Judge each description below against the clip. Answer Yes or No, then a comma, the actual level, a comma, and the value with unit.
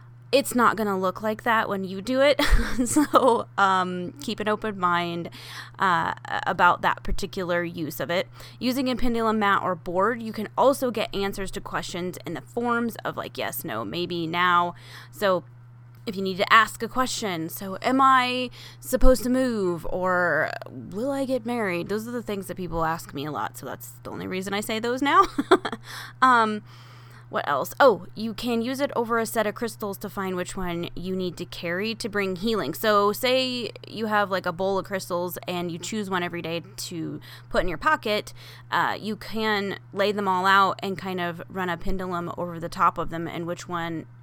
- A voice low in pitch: No, high, 190 Hz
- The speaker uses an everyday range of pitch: Yes, average, 4.6 semitones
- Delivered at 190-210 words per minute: Yes, average, 200 wpm